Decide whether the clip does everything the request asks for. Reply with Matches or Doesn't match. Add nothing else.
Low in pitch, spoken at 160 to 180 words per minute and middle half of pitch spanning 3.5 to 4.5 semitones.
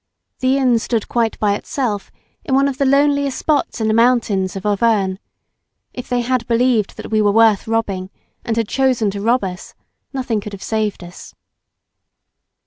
Doesn't match